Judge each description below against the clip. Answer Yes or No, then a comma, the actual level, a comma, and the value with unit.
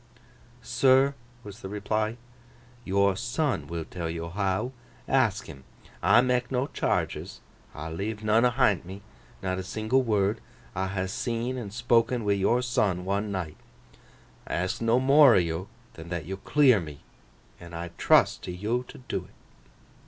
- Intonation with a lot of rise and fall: No, average, 4.7 semitones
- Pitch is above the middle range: No, low, 105 Hz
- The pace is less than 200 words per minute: Yes, average, 160 wpm